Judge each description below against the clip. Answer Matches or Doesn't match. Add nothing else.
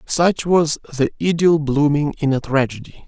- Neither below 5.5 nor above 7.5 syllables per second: Doesn't match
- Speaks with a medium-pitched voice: Matches